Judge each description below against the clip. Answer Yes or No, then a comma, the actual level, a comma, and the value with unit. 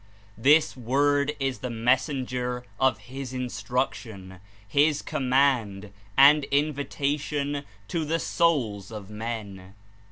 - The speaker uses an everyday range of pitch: Yes, average, 4.0 semitones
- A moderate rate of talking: No, slow, 105 wpm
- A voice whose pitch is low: Yes, low, 130 Hz